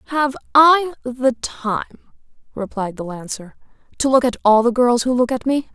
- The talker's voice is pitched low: No, high, 245 Hz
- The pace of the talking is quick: No, average, 180 wpm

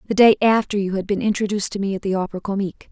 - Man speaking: No, female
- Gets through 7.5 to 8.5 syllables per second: Yes, 7.9 syllables/s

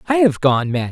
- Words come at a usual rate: No, fast, 260 wpm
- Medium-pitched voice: Yes, medium, 150 Hz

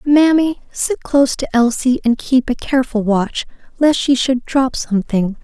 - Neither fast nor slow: Yes, average, 165 wpm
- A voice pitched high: Yes, very high, 255 Hz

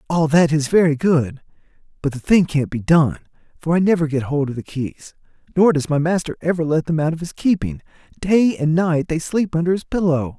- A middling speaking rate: No, fast, 220 wpm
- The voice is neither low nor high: Yes, medium, 160 Hz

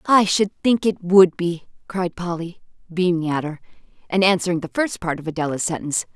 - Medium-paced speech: Yes, average, 185 wpm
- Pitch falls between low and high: Yes, medium, 180 Hz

